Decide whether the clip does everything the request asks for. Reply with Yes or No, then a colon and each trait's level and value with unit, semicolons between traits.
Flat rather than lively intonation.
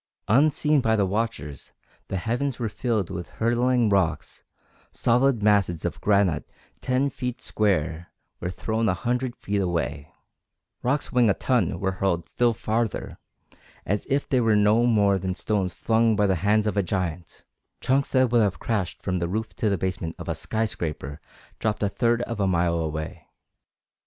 No: average, 4.3 semitones